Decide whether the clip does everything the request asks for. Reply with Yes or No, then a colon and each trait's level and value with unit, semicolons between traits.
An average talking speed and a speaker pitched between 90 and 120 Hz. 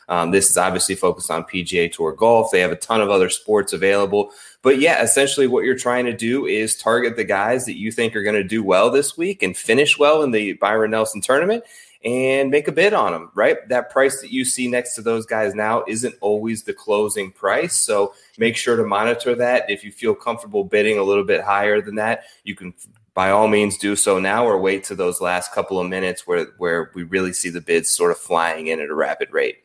No: fast, 235 wpm; low, 115 Hz